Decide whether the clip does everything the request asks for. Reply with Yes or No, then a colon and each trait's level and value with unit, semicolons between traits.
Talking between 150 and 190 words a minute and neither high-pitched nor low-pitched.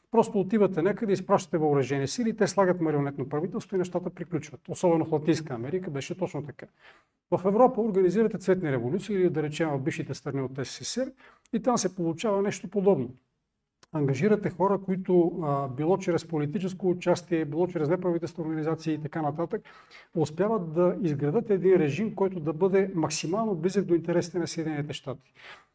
Yes: average, 160 wpm; medium, 175 Hz